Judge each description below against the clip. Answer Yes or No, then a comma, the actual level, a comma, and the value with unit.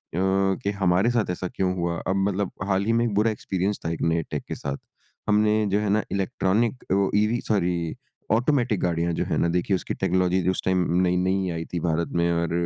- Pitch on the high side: No, very low, 95 Hz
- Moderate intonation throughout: Yes, average, 3.1 semitones